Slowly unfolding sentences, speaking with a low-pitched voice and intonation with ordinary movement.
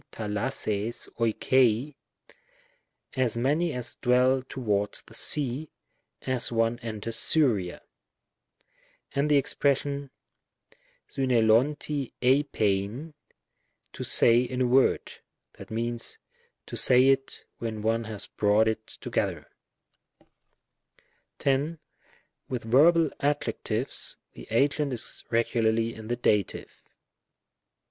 Yes: slow, 100 wpm; low, 125 Hz; average, 3.9 semitones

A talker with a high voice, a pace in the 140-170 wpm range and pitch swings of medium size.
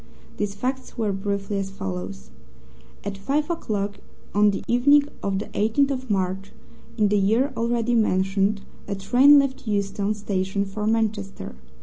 Yes: high, 205 Hz; average, 145 wpm; average, 3.3 semitones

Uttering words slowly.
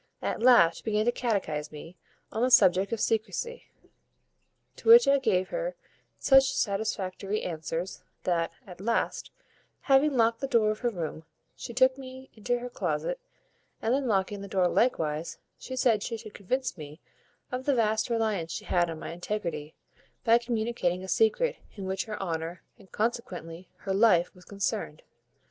No: average, 165 wpm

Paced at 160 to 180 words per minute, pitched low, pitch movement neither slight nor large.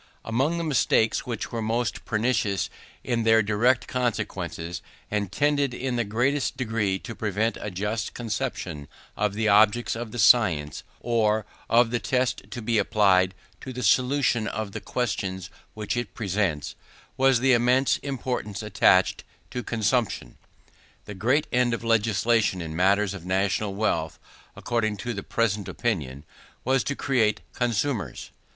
No: average, 145 wpm; low, 110 Hz; average, 3.4 semitones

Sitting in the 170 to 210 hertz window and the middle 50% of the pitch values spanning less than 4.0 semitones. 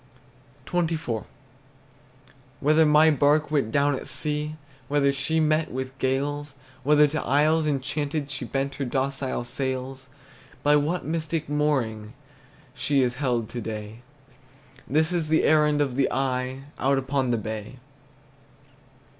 No: medium, 140 Hz; narrow, 2.6 semitones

